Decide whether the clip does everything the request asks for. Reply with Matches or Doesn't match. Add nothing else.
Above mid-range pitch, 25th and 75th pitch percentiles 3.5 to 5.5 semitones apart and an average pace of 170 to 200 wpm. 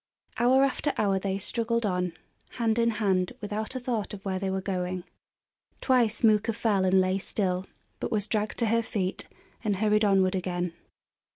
Doesn't match